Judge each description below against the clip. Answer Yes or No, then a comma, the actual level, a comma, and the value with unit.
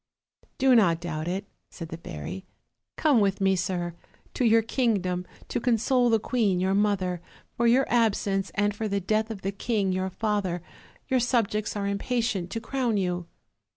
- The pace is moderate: Yes, average, 170 wpm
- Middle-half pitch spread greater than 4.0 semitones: No, average, 3.7 semitones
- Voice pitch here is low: No, high, 200 Hz